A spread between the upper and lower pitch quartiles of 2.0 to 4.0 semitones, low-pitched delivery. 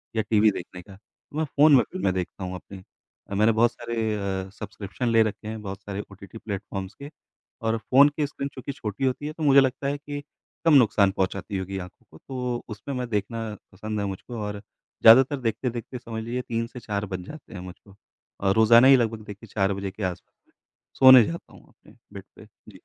No: average, 4.4 semitones; low, 110 Hz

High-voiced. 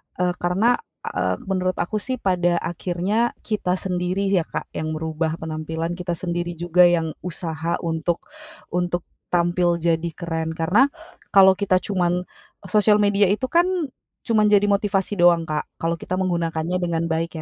No: medium, 175 Hz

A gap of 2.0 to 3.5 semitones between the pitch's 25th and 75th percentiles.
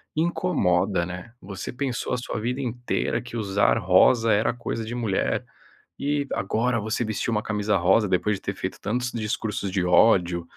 No: average, 4.1 semitones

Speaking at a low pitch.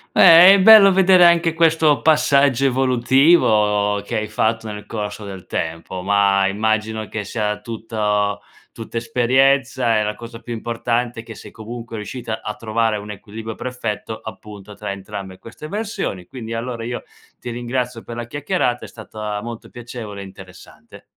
Yes: low, 115 Hz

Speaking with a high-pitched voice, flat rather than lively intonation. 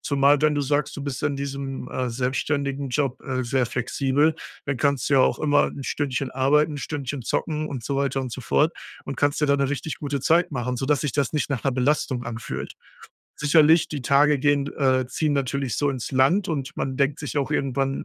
No: medium, 140 Hz; narrow, 1.9 semitones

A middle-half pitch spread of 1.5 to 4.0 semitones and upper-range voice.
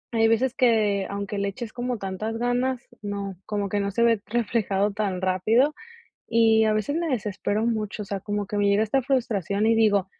Yes: narrow, 2.6 semitones; high, 215 Hz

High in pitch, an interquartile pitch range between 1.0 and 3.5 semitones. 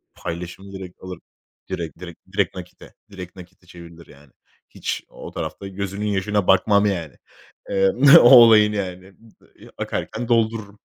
No: very low, 95 Hz; average, 2.9 semitones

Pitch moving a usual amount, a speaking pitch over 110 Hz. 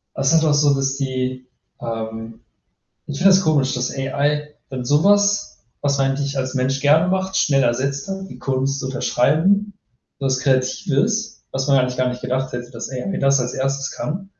Yes: average, 3.0 semitones; low, 135 Hz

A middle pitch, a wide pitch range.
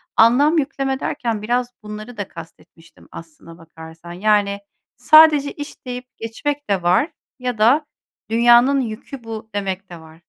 No: high, 225 Hz; wide, 5.7 semitones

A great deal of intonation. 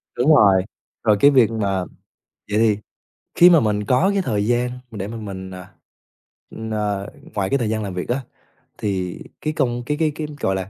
No: average, 4.6 semitones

